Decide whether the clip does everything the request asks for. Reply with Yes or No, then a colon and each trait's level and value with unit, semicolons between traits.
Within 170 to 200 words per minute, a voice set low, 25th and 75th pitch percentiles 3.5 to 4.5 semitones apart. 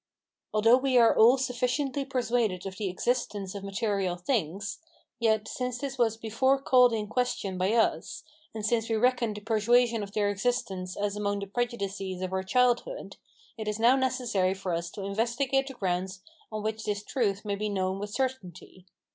No: average, 180 wpm; high, 215 Hz; average, 3.8 semitones